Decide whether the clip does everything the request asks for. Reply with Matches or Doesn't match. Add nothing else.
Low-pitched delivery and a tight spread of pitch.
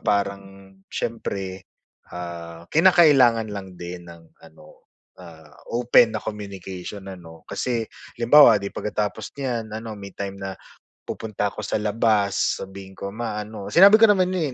Doesn't match